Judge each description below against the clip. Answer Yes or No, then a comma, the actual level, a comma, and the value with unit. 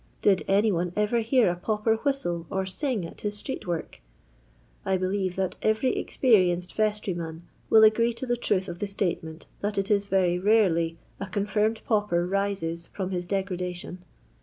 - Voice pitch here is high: Yes, high, 195 Hz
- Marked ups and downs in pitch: No, average, 3.2 semitones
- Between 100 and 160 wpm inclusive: No, average, 170 wpm